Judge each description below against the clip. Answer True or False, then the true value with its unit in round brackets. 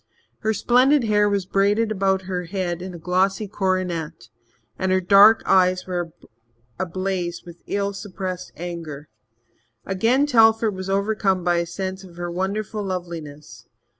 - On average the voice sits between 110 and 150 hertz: False (190 Hz)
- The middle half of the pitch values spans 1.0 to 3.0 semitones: True (2.5 semitones)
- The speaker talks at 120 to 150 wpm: True (140 wpm)